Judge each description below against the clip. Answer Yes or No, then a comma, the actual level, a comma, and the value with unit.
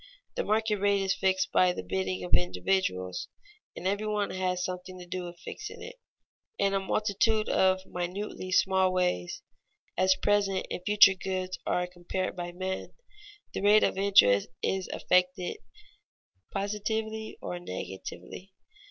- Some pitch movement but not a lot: No, narrow, 2.1 semitones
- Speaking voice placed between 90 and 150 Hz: No, medium, 185 Hz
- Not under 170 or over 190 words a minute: No, average, 145 wpm